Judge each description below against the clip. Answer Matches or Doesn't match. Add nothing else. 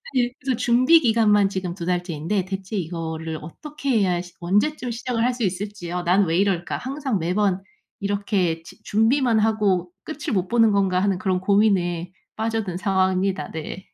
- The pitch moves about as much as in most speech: Matches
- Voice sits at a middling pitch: Doesn't match